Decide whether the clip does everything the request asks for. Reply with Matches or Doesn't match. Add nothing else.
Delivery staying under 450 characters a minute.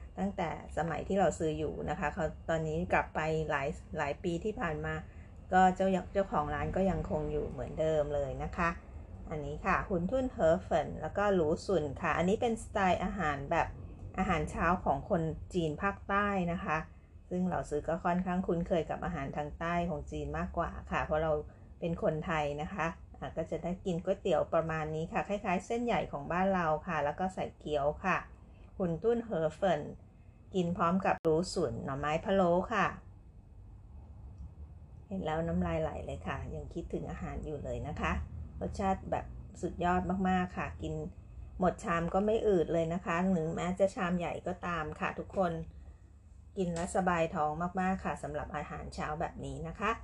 Doesn't match